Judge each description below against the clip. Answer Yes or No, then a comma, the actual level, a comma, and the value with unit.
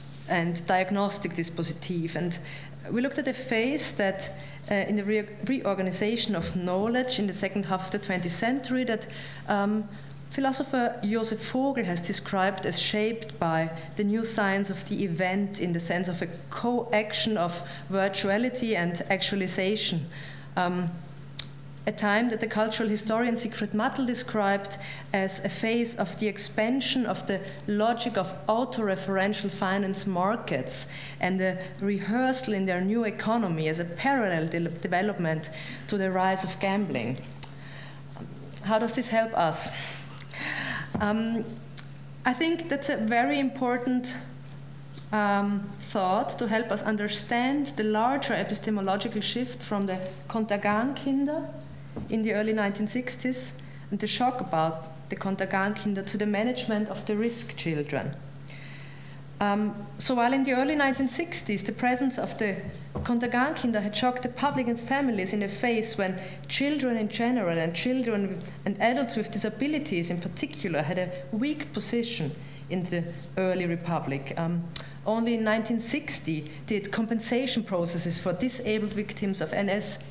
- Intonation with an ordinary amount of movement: Yes, average, 4.8 semitones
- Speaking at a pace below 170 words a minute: Yes, average, 145 wpm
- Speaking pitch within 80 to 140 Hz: No, high, 200 Hz